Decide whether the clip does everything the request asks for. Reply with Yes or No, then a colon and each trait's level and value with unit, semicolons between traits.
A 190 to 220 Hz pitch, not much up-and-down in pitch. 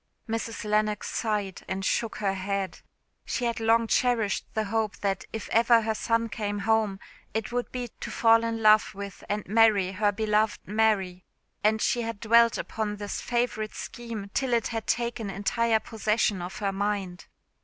Yes: high, 215 Hz; narrow, 2.1 semitones